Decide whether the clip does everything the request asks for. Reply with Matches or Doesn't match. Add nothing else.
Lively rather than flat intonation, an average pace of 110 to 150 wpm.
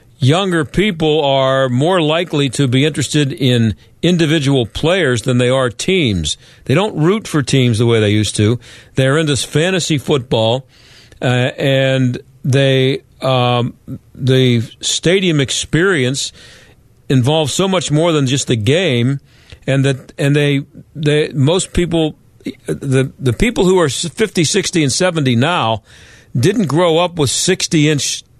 Doesn't match